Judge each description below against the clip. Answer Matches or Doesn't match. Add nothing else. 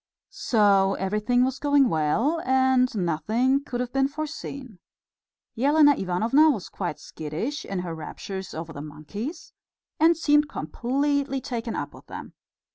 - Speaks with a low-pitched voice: Doesn't match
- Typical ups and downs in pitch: Doesn't match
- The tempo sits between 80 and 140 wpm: Matches